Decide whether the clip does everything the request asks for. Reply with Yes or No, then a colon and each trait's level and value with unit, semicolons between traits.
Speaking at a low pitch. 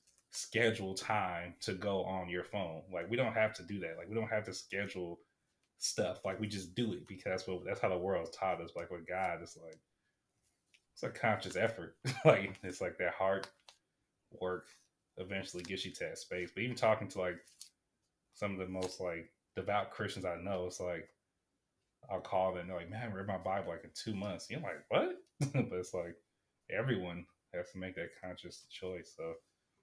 Yes: very low, 95 Hz